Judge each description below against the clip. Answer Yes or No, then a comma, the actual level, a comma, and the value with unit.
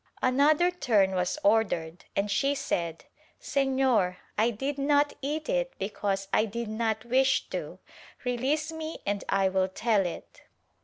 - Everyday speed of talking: Yes, average, 150 wpm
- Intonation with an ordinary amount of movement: No, wide, 6.2 semitones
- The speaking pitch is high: Yes, high, 235 Hz